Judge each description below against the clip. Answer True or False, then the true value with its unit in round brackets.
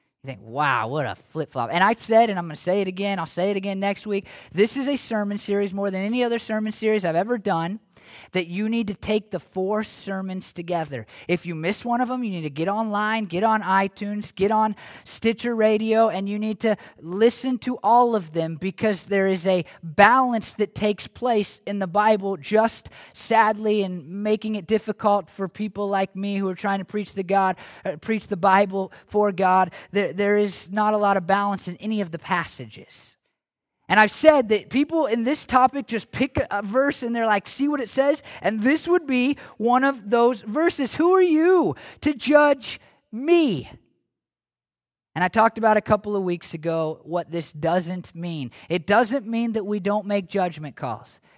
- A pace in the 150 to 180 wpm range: False (200 wpm)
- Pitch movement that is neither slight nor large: True (3.4 semitones)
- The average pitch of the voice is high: True (205 Hz)